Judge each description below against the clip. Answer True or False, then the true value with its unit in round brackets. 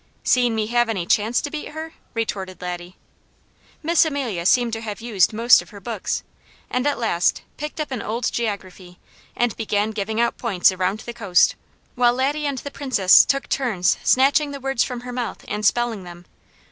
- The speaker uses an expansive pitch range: False (4.4 semitones)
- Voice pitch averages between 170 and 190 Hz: False (230 Hz)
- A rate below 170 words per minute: False (185 wpm)